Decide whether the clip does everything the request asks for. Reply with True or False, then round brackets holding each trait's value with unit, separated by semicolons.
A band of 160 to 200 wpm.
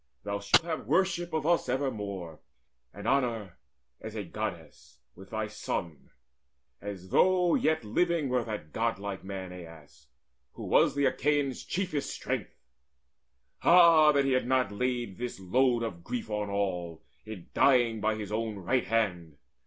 False (150 wpm)